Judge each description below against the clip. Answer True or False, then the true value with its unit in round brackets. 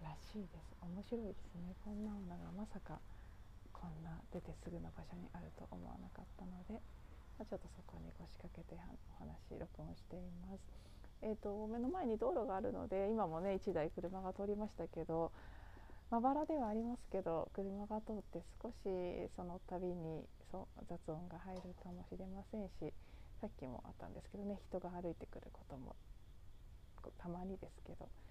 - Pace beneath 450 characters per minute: True (340 characters per minute)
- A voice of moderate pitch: True (175 Hz)